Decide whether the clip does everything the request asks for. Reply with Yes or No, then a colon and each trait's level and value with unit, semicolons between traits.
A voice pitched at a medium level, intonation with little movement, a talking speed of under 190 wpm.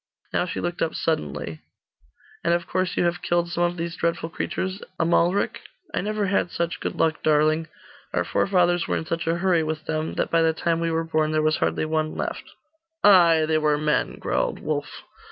No: medium, 165 Hz; narrow, 1.8 semitones; average, 200 wpm